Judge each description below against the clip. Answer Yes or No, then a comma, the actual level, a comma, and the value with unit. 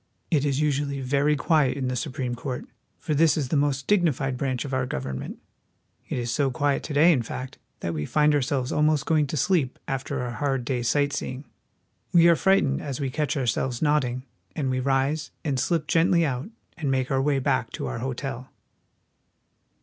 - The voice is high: No, medium, 140 Hz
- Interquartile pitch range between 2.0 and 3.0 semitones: Yes, average, 2.7 semitones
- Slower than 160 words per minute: No, average, 195 wpm